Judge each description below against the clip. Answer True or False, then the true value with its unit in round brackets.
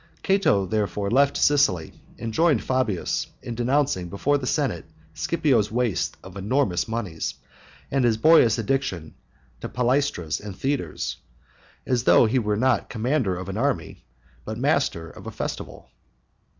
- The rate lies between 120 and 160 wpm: True (140 wpm)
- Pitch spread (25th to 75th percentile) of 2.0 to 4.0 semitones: False (5.6 semitones)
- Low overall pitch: True (115 Hz)